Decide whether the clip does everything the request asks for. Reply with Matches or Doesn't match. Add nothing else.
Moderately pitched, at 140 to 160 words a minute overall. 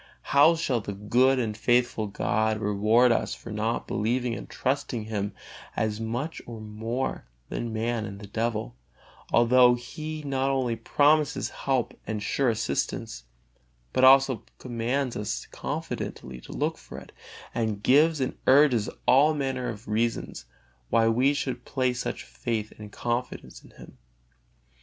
Doesn't match